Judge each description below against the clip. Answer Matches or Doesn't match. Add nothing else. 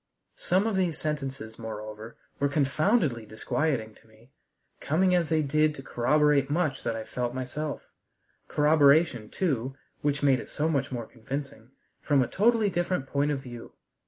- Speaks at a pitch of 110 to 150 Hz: Matches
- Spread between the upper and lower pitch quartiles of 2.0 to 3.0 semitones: Doesn't match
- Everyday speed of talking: Matches